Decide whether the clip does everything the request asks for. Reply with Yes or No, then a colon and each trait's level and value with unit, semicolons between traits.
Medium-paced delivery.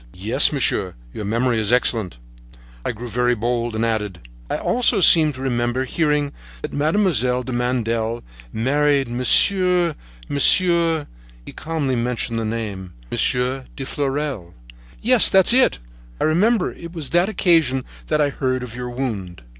Yes: average, 145 wpm